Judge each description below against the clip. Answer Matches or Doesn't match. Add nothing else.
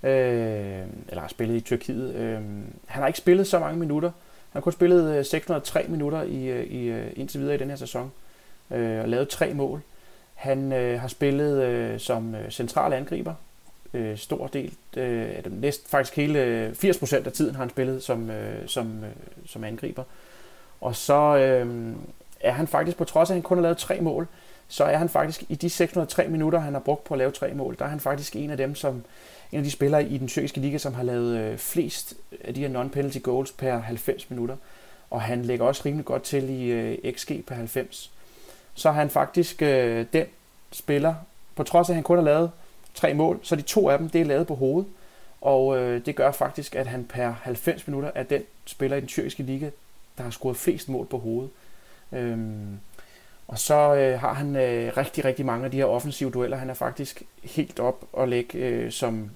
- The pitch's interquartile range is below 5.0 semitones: Matches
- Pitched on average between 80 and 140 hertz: Matches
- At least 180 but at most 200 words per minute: Matches